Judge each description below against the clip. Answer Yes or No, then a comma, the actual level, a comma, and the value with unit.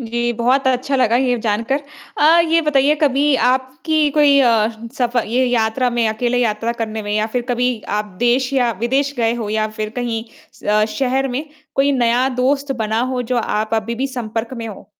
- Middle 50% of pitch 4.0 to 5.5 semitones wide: No, average, 2.9 semitones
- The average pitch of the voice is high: Yes, high, 245 Hz